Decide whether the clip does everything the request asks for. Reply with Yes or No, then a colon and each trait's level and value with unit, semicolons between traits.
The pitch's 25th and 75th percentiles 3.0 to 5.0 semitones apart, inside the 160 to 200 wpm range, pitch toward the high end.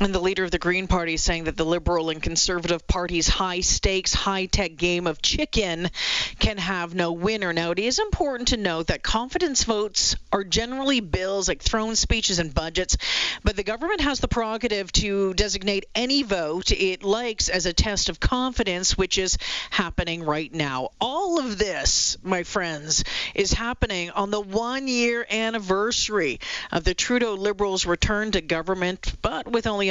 Yes: average, 4.1 semitones; average, 175 wpm; high, 195 Hz